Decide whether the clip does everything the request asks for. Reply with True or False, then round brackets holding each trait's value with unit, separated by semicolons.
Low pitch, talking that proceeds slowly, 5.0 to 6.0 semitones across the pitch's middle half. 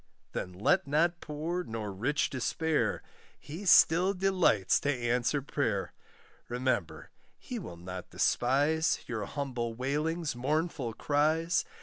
False (145 Hz; 115 wpm; 5.4 semitones)